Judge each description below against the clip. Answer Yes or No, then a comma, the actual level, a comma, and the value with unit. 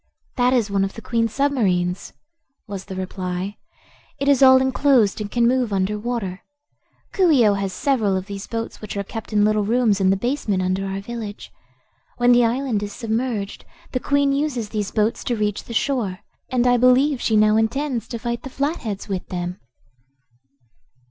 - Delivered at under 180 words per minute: No, average, 185 wpm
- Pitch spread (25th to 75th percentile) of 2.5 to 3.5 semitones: No, average, 4.1 semitones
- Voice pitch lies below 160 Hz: No, high, 225 Hz